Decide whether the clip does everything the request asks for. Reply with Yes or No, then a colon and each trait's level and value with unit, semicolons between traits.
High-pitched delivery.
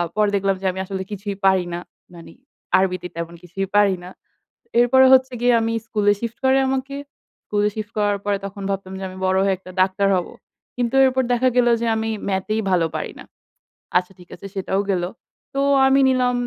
Yes: high, 200 Hz